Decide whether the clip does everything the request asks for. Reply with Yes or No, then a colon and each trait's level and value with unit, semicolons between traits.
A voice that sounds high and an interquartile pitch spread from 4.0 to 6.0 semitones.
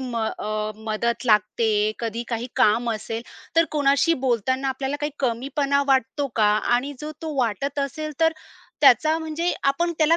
Yes: very high, 265 Hz; average, 4.5 semitones